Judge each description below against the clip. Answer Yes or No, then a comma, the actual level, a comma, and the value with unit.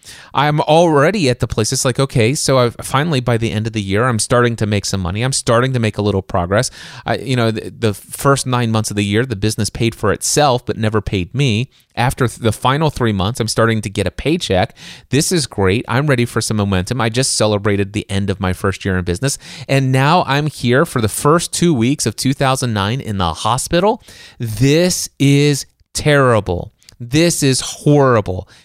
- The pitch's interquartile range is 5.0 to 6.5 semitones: No, average, 4.2 semitones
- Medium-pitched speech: No, low, 120 Hz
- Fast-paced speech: Yes, fast, 215 wpm